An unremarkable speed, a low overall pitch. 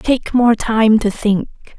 No: average, 170 wpm; high, 220 Hz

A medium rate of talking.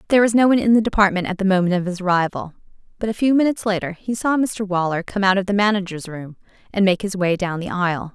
No: fast, 260 wpm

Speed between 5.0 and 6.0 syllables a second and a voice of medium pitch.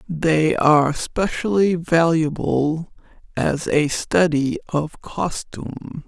No: 3.2 syllables/s; medium, 160 Hz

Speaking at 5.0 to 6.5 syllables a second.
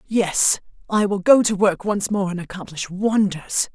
No: 4.3 syllables/s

